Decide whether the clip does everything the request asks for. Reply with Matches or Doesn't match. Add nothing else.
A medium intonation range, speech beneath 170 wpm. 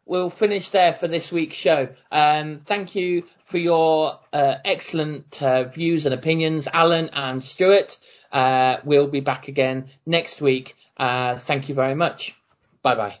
Matches